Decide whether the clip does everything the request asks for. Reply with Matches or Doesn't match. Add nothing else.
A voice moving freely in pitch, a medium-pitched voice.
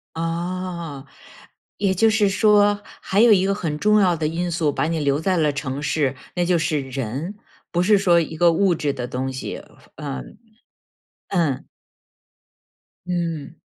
Doesn't match